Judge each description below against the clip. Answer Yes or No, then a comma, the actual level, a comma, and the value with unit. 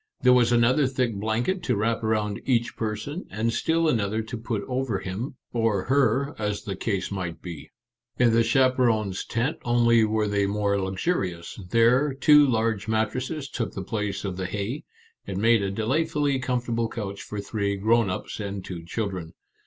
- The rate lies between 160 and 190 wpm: Yes, average, 175 wpm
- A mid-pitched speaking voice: No, low, 110 Hz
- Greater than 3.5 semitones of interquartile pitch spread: Yes, average, 3.9 semitones